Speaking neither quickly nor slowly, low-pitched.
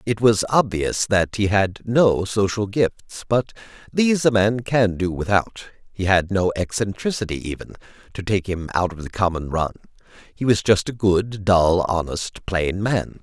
Yes: average, 170 wpm; low, 100 Hz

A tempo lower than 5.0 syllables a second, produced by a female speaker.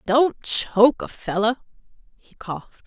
Yes: 4.7 syllables/s; female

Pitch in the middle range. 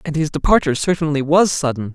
Yes: medium, 150 Hz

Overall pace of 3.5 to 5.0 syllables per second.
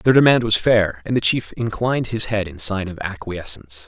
No: 5.3 syllables/s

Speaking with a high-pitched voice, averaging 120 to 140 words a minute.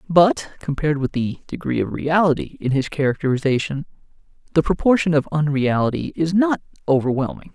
No: medium, 150 Hz; slow, 135 wpm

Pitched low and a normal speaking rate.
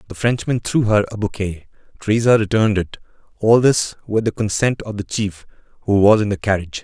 Yes: low, 105 Hz; average, 185 wpm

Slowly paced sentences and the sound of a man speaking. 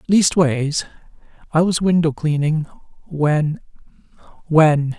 Yes: slow, 70 wpm; male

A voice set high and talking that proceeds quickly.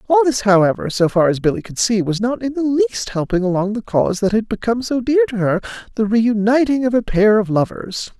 Yes: high, 220 Hz; fast, 225 wpm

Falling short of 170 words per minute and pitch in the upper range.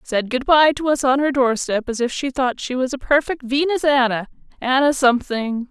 No: average, 200 wpm; very high, 260 Hz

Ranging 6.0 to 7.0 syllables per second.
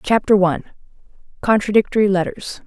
Yes: 6.2 syllables/s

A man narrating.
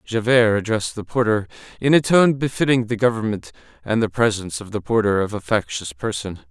Yes: male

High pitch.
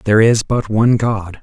No: low, 110 Hz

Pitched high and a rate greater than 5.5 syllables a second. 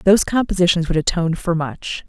No: medium, 175 Hz; 5.9 syllables/s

